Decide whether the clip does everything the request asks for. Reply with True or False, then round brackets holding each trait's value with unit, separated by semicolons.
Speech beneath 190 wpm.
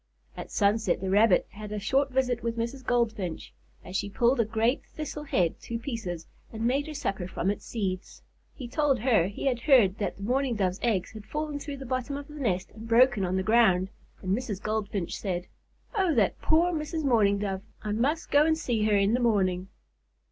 False (205 wpm)